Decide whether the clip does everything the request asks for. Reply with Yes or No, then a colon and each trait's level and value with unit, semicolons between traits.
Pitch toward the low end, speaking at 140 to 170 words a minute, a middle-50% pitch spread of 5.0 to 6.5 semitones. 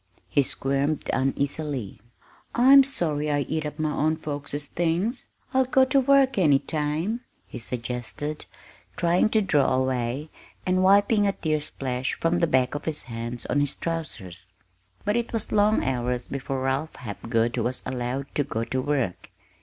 No: medium, 145 Hz; average, 160 wpm; average, 5.3 semitones